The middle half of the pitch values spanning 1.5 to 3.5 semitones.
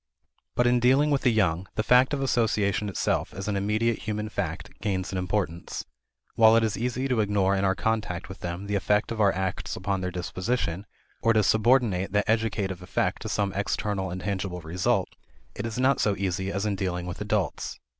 Yes: average, 3.1 semitones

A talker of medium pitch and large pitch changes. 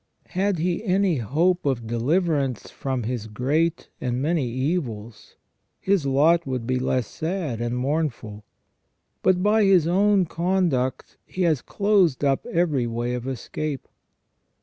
Yes: medium, 145 Hz; wide, 6.1 semitones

